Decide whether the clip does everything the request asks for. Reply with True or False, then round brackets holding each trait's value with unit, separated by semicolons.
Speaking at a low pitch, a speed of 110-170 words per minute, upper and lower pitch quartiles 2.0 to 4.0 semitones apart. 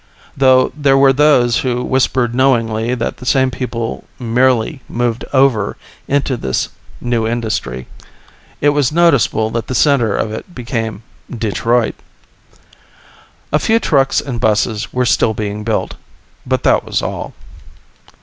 True (120 Hz; 135 wpm; 3.1 semitones)